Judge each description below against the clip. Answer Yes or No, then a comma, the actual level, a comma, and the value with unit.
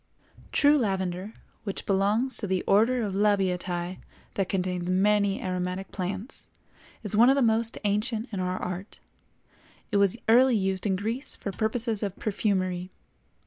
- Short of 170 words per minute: Yes, average, 145 wpm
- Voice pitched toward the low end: No, high, 200 Hz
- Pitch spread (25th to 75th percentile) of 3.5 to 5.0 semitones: No, average, 3.1 semitones